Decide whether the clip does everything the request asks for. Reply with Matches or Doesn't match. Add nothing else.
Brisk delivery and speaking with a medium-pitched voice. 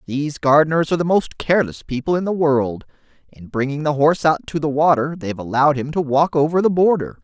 Matches